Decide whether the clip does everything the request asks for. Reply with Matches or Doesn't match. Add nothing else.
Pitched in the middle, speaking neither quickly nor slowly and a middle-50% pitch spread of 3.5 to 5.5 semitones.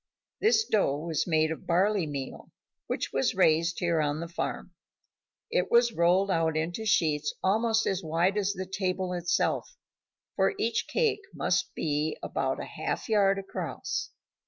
Matches